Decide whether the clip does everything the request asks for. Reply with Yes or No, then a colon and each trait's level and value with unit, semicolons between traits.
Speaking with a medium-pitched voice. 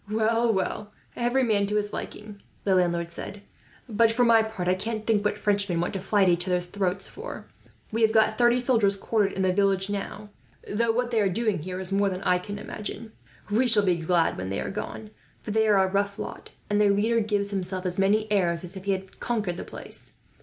No: high, 205 Hz